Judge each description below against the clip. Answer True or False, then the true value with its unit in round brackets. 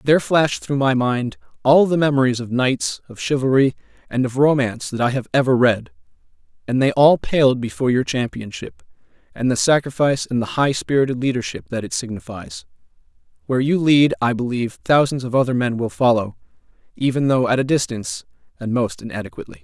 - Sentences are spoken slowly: False (175 wpm)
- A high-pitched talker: False (130 Hz)